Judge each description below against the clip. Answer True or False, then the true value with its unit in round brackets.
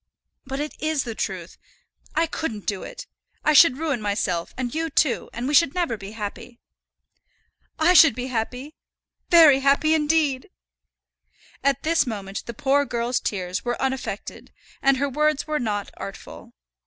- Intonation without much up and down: False (5.0 semitones)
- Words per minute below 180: True (155 wpm)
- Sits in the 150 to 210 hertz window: False (270 Hz)